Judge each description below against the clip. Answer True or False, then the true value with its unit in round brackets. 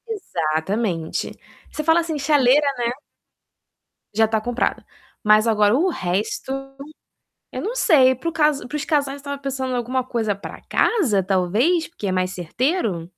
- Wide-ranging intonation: True (6.6 semitones)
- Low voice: False (250 Hz)